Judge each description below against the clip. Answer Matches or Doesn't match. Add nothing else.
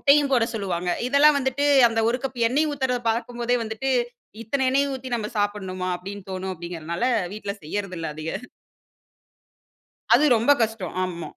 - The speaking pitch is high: Matches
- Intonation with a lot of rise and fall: Matches